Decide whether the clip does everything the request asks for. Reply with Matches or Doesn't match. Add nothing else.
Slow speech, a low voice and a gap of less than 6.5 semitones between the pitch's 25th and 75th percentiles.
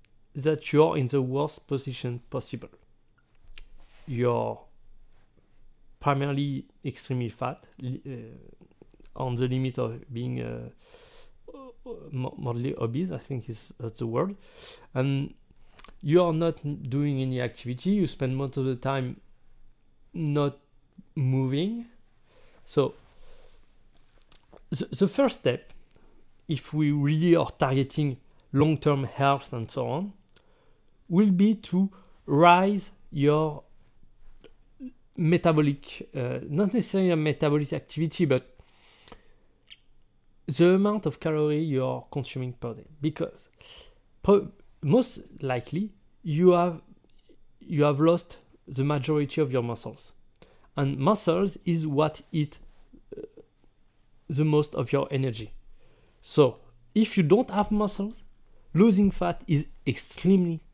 Doesn't match